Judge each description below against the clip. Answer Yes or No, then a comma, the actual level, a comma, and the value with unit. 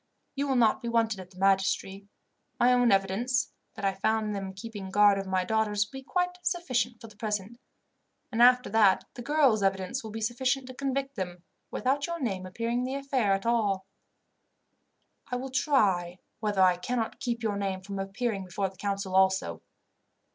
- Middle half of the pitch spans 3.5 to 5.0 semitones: Yes, average, 4.4 semitones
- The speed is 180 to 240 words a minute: Yes, average, 185 wpm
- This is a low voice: No, high, 220 Hz